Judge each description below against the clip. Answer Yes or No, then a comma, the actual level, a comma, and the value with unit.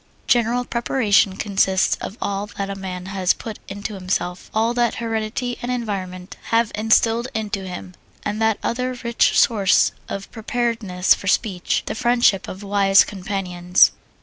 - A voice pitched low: No, high, 205 Hz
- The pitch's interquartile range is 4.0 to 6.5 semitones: No, average, 3.3 semitones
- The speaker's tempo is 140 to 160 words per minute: Yes, average, 150 wpm